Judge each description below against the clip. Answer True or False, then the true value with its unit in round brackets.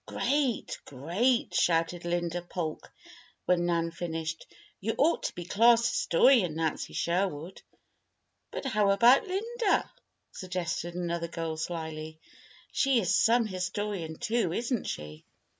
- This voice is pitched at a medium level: True (180 Hz)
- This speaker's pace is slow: True (120 wpm)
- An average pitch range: False (5.8 semitones)